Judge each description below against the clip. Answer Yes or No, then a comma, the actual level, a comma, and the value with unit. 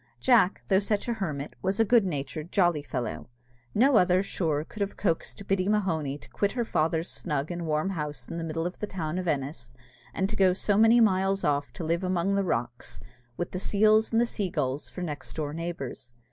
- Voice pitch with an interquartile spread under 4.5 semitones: No, average, 4.8 semitones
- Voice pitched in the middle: Yes, medium, 175 Hz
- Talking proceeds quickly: Yes, fast, 215 wpm